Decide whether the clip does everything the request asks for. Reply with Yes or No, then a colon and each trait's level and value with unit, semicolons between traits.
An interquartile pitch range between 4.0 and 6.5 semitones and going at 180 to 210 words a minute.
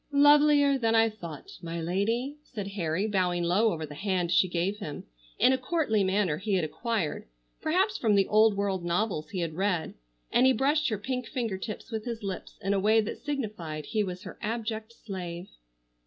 Yes: average, 4.5 semitones; average, 195 wpm